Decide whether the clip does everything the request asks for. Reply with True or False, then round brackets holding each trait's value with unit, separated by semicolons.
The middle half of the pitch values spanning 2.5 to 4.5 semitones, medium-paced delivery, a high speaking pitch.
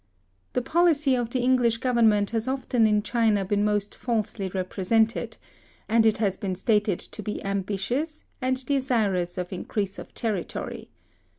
True (3.8 semitones; 150 wpm; 220 Hz)